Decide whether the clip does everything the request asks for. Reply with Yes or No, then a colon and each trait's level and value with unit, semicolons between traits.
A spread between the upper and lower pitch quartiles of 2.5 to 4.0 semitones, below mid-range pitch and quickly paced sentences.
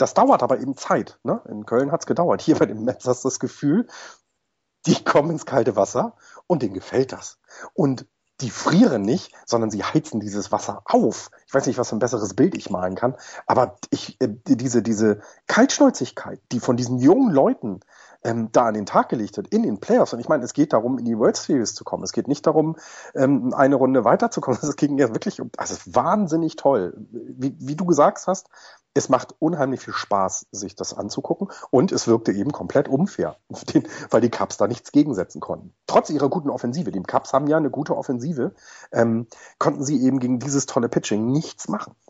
No: average, 4.5 semitones; low, 130 Hz; fast, 200 wpm